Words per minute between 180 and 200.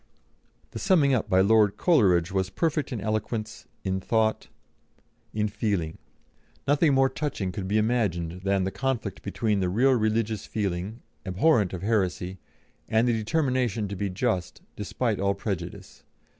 No: average, 145 wpm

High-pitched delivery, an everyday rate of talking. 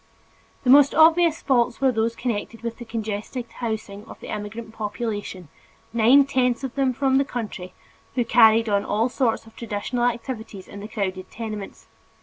Yes: high, 230 Hz; average, 165 wpm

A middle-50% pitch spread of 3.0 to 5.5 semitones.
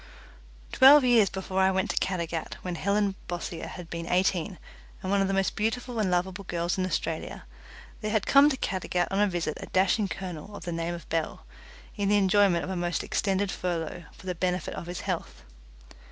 No: narrow, 2.5 semitones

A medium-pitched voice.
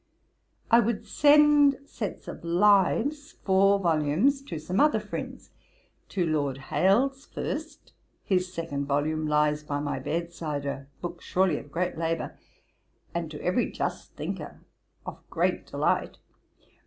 Yes: medium, 175 Hz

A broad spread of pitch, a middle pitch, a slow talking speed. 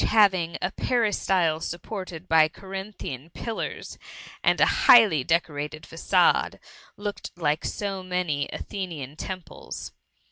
No: average, 3.8 semitones; medium, 180 Hz; slow, 105 wpm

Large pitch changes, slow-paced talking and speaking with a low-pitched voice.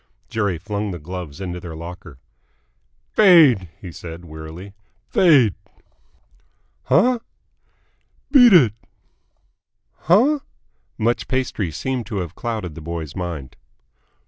Yes: wide, 7.0 semitones; slow, 105 wpm; very low, 95 Hz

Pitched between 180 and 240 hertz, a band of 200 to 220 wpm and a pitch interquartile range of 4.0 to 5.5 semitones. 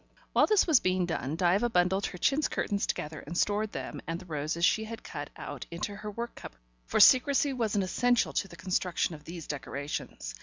Yes: medium, 185 Hz; fast, 205 wpm; average, 4.9 semitones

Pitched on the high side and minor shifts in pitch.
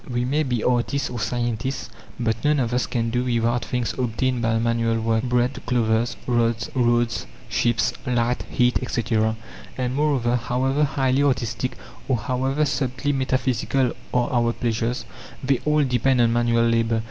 No: low, 120 Hz; narrow, 1.8 semitones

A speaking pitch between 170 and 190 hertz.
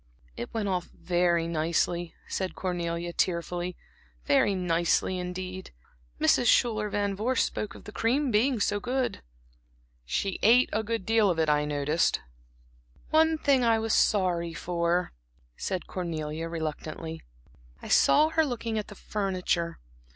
Yes: medium, 185 Hz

